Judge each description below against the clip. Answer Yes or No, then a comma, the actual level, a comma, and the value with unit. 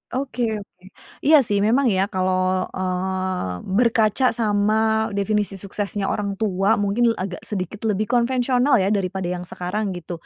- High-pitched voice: Yes, high, 200 Hz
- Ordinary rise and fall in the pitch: Yes, average, 3.0 semitones